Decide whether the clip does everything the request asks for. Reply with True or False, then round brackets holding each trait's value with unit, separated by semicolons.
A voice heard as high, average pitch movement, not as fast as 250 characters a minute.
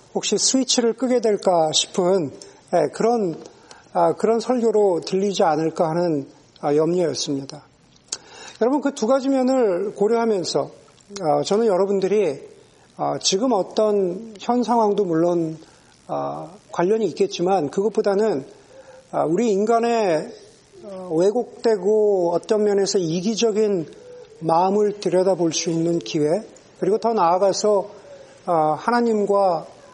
True (200 Hz; 4.5 semitones; 235 characters per minute)